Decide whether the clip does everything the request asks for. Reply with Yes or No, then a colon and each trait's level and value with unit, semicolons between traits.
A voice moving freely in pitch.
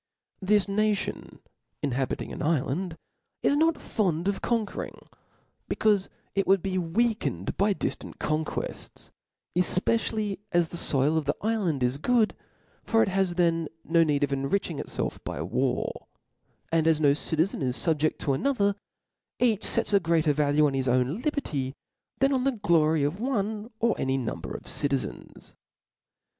Yes: wide, 6.3 semitones